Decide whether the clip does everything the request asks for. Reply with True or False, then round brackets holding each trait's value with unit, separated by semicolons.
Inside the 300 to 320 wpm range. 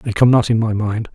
True (315 wpm)